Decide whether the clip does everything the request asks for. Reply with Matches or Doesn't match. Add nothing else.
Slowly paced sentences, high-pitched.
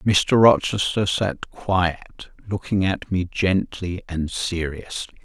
Doesn't match